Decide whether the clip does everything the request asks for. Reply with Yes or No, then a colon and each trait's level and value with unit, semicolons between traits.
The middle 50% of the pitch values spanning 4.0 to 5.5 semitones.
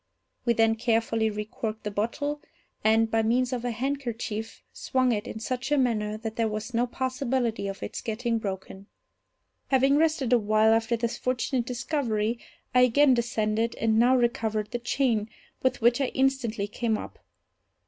No: narrow, 2.5 semitones